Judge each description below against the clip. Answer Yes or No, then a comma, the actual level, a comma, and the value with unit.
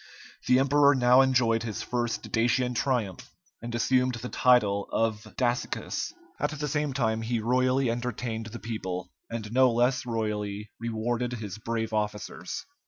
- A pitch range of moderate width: No, narrow, 2.3 semitones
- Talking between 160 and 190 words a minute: No, average, 145 wpm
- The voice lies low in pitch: Yes, low, 120 Hz